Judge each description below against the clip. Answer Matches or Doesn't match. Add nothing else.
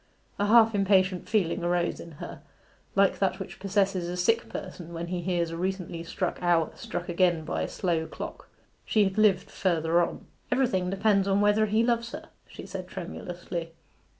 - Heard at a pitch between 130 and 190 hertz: Matches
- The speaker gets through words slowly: Doesn't match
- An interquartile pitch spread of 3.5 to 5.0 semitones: Doesn't match